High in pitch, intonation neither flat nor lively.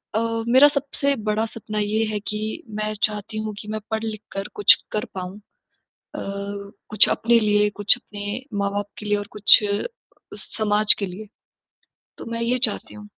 No: high, 210 Hz; narrow, 1.4 semitones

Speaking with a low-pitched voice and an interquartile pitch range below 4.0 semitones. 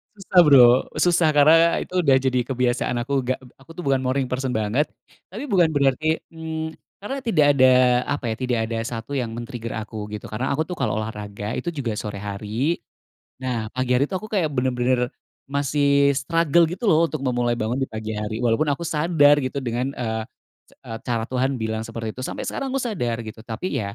No: low, 130 Hz; average, 5.2 semitones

